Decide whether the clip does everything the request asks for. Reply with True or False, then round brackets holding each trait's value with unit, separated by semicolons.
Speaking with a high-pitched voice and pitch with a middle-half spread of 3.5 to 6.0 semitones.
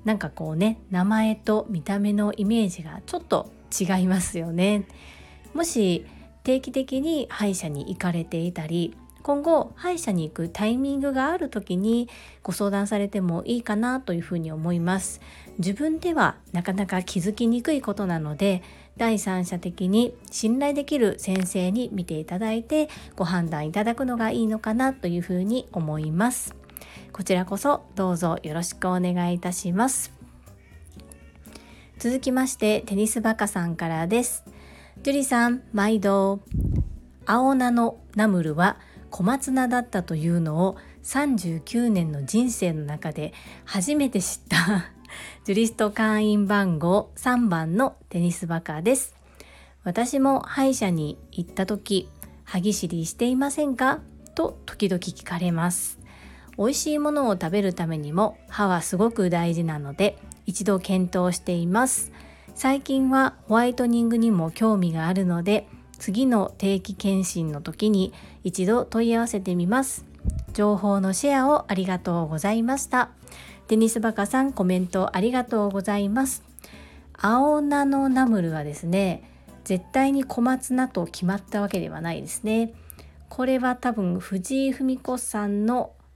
True (200 Hz; 5.3 semitones)